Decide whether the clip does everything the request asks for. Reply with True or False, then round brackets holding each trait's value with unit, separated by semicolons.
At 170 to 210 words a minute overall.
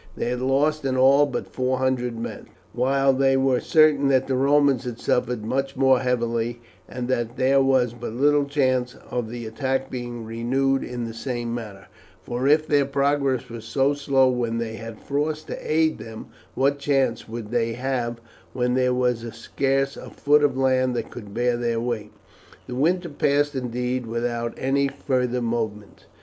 True (175 wpm)